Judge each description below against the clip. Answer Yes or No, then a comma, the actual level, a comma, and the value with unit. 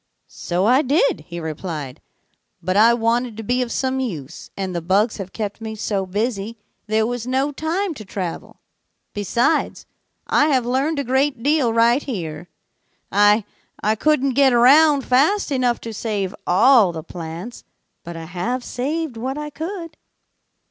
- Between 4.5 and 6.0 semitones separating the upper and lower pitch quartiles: Yes, wide, 5.6 semitones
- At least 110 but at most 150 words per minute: No, average, 160 wpm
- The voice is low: No, high, 235 Hz